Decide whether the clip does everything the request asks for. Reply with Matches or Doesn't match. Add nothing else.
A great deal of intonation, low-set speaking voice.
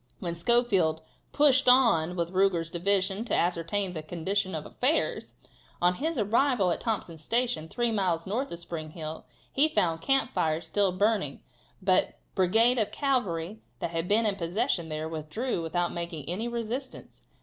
Doesn't match